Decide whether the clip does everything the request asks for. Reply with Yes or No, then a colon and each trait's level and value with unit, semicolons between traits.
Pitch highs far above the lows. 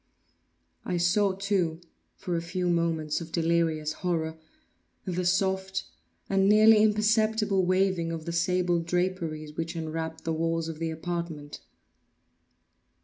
No: average, 2.7 semitones